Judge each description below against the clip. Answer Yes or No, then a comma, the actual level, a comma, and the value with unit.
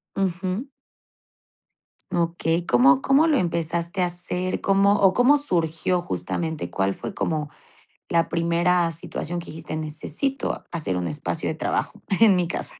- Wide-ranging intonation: No, narrow, 2.6 semitones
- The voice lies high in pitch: No, medium, 170 Hz